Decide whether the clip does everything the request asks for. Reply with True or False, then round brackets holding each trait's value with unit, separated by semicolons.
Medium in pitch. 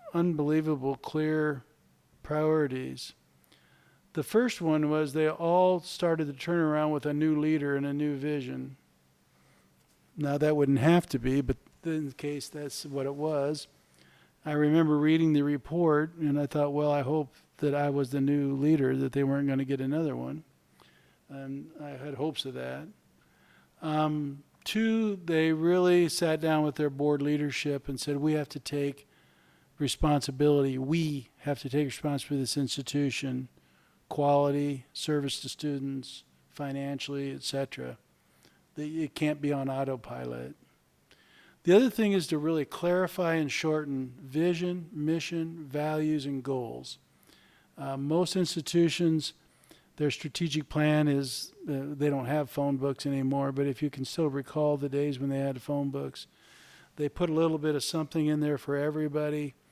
True (145 Hz)